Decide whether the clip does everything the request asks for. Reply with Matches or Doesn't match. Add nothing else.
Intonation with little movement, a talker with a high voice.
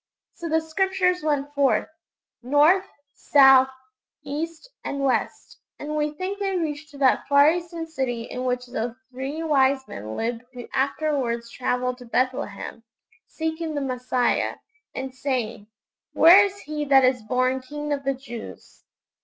Doesn't match